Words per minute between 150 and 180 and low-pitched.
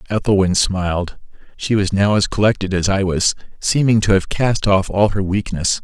Yes: average, 175 wpm; low, 100 Hz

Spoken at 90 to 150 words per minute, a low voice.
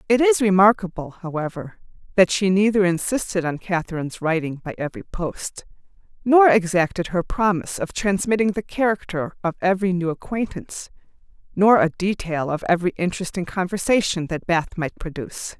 No: average, 140 wpm; medium, 185 Hz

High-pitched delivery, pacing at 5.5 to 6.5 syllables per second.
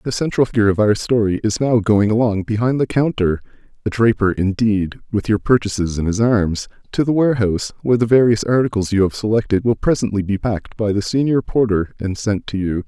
No: low, 110 Hz; 5.9 syllables/s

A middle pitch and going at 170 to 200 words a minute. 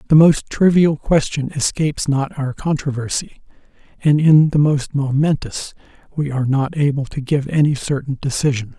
No: medium, 145 Hz; average, 150 wpm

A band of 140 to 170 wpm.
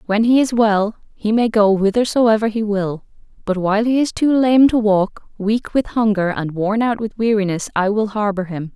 No: fast, 205 wpm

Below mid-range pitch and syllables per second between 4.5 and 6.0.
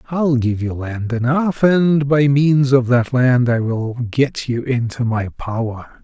No: low, 125 Hz; 3.6 syllables/s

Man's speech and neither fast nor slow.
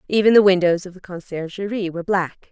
No: female; average, 190 wpm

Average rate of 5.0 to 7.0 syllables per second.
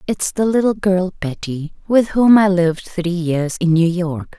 No: 4.3 syllables/s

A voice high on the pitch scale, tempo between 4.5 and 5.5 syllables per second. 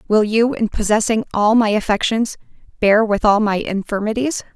Yes: high, 215 Hz; 5.0 syllables/s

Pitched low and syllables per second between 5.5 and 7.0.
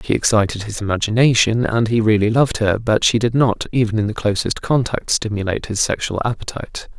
Yes: low, 110 Hz; 5.9 syllables/s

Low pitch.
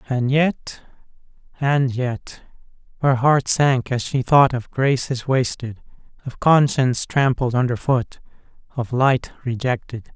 Yes: low, 130 Hz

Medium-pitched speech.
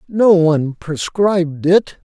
Yes: medium, 170 Hz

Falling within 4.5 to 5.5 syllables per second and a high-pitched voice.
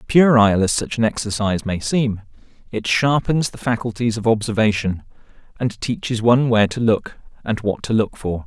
No: 5.4 syllables/s; low, 110 Hz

